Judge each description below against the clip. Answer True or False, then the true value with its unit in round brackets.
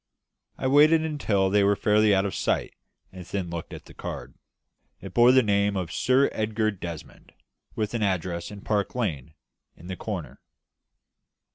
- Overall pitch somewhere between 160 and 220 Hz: False (100 Hz)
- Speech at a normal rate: True (165 wpm)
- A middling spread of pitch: True (3.4 semitones)